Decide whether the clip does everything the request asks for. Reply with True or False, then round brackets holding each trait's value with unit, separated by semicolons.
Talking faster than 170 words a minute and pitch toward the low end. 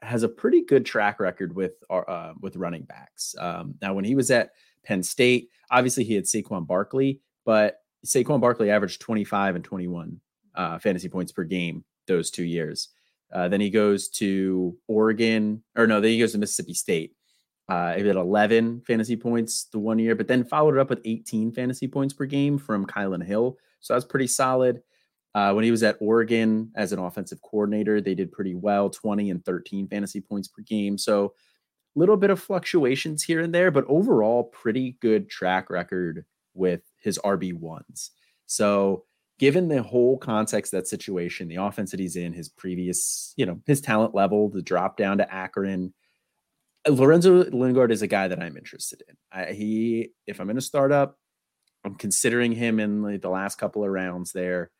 True (190 wpm; 105 Hz)